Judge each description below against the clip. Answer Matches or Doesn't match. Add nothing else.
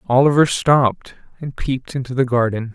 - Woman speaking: Doesn't match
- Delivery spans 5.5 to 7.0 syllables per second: Matches